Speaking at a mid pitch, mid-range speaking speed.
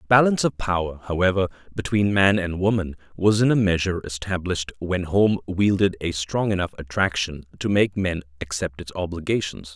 No: very low, 90 Hz; average, 160 wpm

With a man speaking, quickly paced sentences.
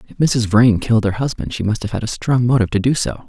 Yes: male; fast, 295 wpm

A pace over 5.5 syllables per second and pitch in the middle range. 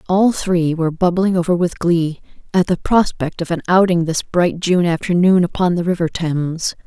No: 4.9 syllables/s; medium, 175 Hz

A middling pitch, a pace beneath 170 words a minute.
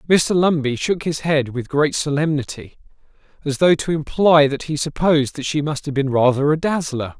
No: medium, 150 Hz; average, 185 wpm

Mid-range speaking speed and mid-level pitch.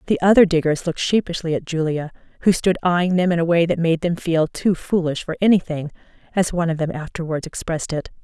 No: fast, 210 wpm; medium, 170 Hz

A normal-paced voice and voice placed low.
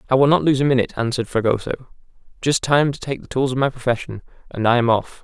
No: fast, 230 wpm; low, 125 Hz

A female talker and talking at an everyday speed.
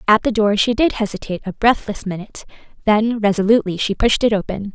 Yes: female; average, 190 wpm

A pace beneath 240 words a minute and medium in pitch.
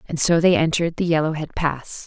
Yes: fast, 205 wpm; medium, 160 Hz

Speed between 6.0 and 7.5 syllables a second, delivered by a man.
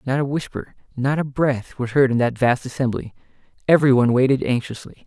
Yes: 6.1 syllables/s; male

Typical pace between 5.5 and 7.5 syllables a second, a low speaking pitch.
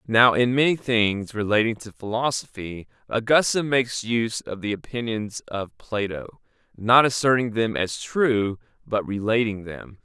No: 4.5 syllables/s; low, 115 Hz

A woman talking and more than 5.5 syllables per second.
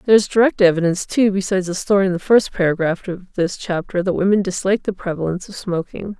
Yes: female; 6.6 syllables/s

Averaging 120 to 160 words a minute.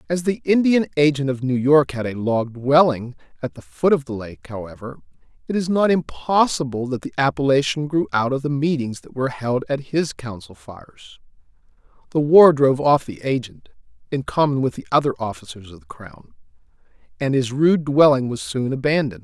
No: average, 185 wpm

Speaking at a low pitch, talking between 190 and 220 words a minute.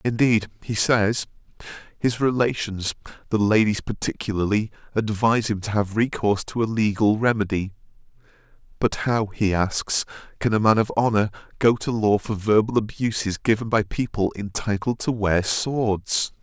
No: low, 110 Hz; average, 140 wpm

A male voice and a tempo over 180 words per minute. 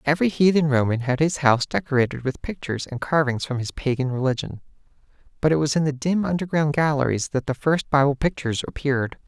Yes: male; average, 190 wpm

